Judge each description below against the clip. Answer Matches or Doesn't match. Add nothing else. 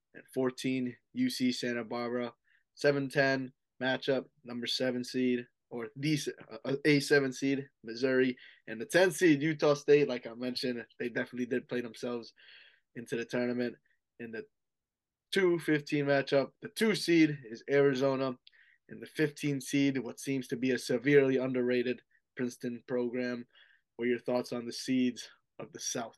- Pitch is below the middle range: Matches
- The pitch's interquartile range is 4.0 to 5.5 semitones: Doesn't match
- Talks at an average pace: Matches